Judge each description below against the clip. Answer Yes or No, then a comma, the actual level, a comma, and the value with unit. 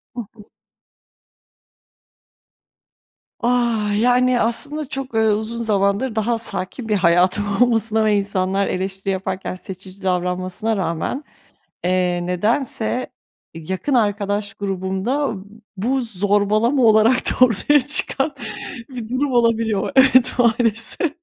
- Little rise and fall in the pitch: No, average, 4.3 semitones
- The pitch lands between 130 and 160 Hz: No, high, 220 Hz